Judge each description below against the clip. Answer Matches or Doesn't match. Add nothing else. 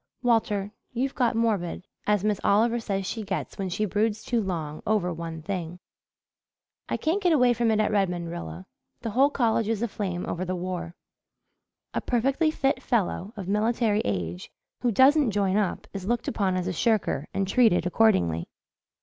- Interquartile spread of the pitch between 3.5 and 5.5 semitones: Matches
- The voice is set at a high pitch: Matches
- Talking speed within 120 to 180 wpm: Matches